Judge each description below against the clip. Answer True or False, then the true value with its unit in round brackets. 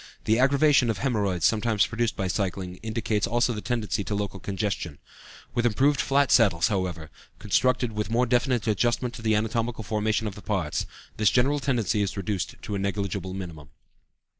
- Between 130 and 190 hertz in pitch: False (110 Hz)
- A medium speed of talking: True (175 wpm)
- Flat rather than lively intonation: False (3.5 semitones)